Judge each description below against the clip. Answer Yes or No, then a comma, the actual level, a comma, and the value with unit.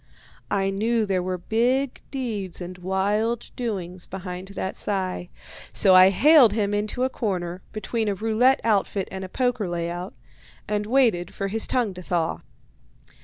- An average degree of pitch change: Yes, average, 3.6 semitones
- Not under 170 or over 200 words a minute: No, average, 155 wpm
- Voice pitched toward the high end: Yes, high, 200 Hz